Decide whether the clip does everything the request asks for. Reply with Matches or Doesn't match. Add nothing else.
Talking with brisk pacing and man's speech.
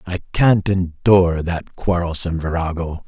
Doesn't match